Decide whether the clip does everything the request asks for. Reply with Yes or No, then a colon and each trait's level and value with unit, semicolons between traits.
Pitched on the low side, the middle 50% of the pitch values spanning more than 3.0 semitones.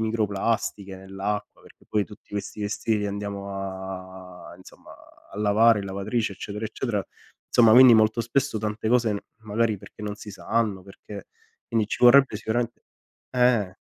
No: low, 105 Hz; narrow, 2.5 semitones